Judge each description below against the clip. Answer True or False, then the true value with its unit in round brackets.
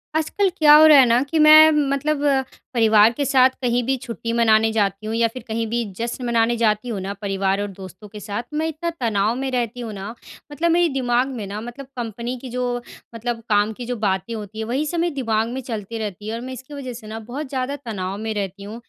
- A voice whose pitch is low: False (235 Hz)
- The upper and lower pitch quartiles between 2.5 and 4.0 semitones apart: True (3.5 semitones)